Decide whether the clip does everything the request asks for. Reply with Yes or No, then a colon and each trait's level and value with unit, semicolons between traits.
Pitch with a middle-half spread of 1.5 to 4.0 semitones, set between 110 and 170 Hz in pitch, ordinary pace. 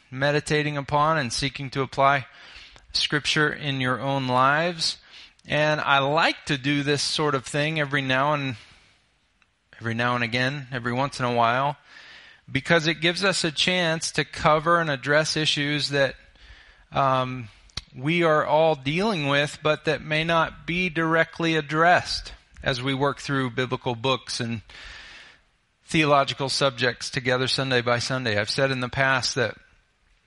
Yes: average, 3.3 semitones; medium, 140 Hz; average, 150 wpm